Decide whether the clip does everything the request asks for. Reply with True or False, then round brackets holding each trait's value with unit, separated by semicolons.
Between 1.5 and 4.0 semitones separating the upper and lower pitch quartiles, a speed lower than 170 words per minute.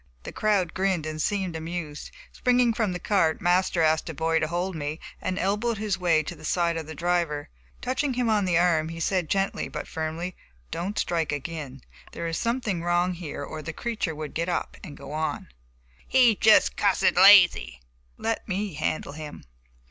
False (3.7 semitones; 185 wpm)